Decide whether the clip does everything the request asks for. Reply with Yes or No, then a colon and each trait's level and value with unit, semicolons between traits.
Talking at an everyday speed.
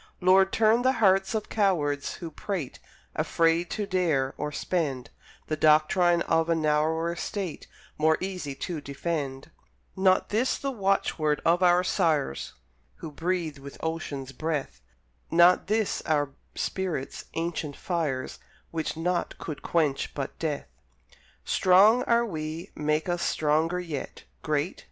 No: slow, 130 wpm